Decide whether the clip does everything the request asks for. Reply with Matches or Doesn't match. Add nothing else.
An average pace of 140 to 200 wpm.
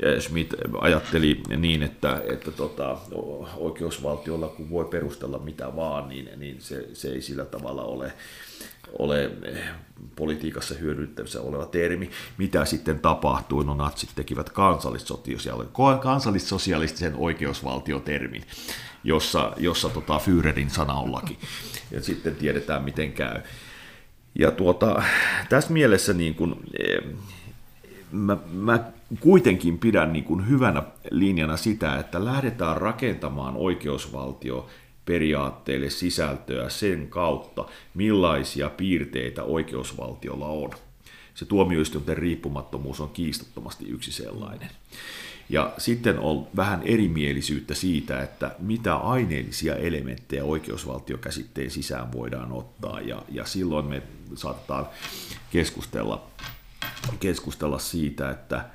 Doesn't match